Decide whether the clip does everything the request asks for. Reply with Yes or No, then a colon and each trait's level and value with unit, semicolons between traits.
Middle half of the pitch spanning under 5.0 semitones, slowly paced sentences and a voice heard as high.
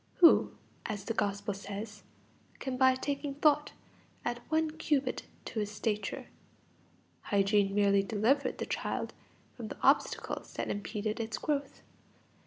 No: wide, 5.5 semitones; slow, 130 wpm; high, 225 Hz